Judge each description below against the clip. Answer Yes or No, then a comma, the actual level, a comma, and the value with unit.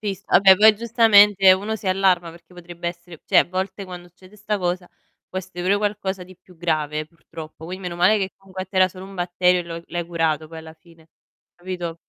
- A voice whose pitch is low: No, medium, 180 Hz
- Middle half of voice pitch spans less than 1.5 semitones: No, narrow, 2.1 semitones